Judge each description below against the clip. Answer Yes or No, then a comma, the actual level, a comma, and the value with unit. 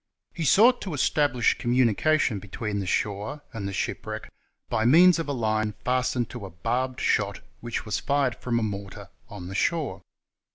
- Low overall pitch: Yes, low, 120 Hz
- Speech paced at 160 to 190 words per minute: Yes, average, 175 wpm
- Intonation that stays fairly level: No, wide, 5.6 semitones